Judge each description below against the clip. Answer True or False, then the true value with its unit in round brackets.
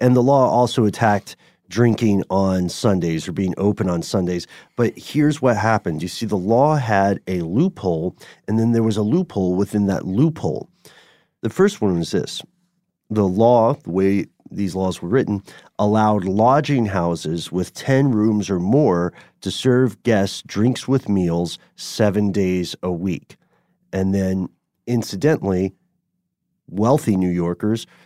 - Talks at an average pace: True (150 wpm)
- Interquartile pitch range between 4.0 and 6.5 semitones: True (4.9 semitones)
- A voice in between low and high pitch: False (105 Hz)